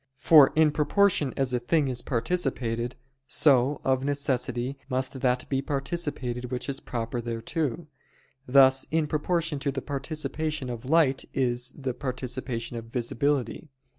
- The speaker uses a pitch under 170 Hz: Yes, low, 135 Hz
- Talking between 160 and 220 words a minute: No, slow, 135 wpm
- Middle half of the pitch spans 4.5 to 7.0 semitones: No, average, 3.1 semitones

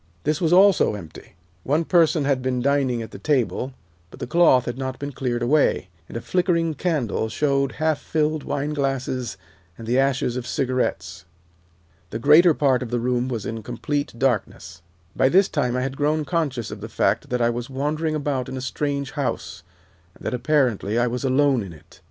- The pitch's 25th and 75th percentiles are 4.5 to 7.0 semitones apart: No, average, 3.5 semitones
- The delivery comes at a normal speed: Yes, average, 190 wpm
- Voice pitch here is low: Yes, low, 130 Hz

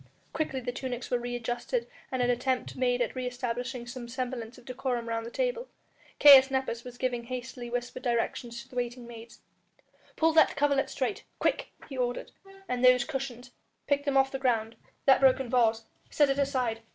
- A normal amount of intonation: No, narrow, 1.9 semitones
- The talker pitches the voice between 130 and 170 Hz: No, very high, 250 Hz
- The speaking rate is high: No, average, 185 wpm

